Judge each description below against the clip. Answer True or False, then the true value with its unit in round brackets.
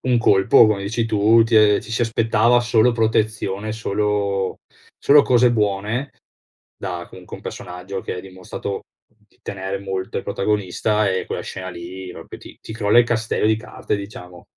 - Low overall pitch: True (105 Hz)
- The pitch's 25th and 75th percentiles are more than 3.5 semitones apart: False (2.7 semitones)